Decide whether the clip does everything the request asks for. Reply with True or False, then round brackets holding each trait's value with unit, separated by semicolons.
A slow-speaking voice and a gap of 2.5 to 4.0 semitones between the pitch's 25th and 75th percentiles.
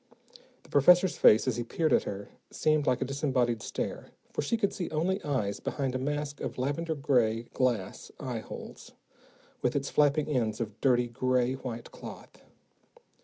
False (165 wpm; 3.6 semitones)